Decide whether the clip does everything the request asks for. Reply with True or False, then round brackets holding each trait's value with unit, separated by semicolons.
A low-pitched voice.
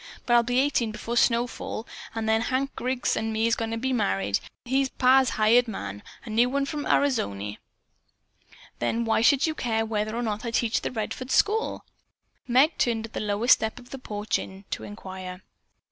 False (230 Hz)